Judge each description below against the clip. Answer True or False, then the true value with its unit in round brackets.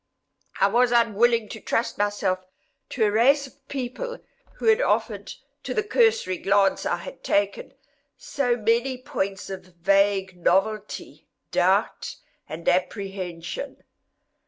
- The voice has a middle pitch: False (215 Hz)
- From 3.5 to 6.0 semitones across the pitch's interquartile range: True (4.9 semitones)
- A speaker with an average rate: False (125 wpm)